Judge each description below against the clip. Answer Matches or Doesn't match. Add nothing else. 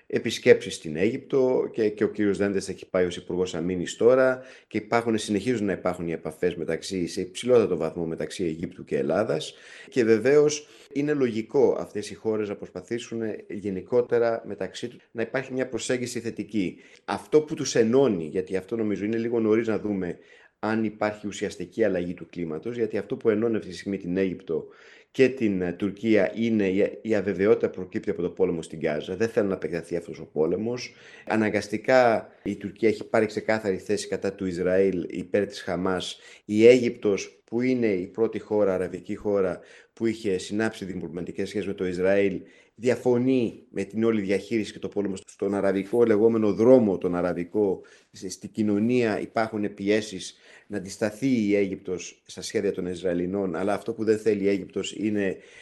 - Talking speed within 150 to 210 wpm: Matches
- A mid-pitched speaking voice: Doesn't match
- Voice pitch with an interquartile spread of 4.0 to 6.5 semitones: Doesn't match